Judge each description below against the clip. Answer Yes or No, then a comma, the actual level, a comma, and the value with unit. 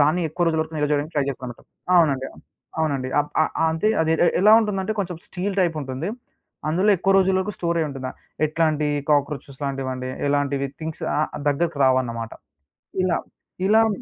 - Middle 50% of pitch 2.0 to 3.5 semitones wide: No, average, 4.0 semitones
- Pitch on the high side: No, medium, 155 Hz